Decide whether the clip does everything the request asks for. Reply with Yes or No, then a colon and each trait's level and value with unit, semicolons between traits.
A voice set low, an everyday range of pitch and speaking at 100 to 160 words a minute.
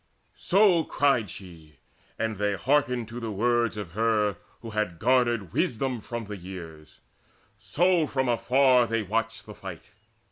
Yes: low, 115 Hz; average, 3.8 semitones; average, 145 wpm